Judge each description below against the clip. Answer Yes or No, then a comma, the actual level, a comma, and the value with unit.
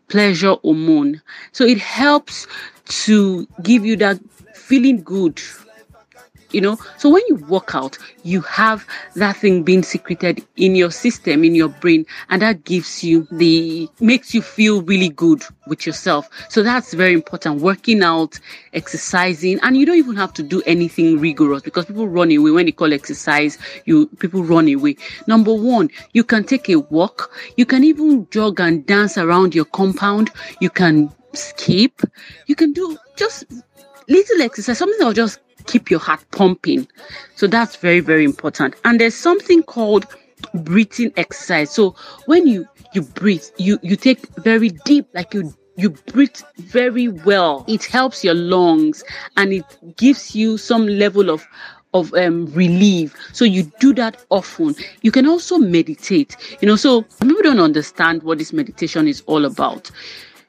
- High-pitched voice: Yes, high, 205 Hz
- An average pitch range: No, wide, 6.6 semitones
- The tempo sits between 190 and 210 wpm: No, average, 165 wpm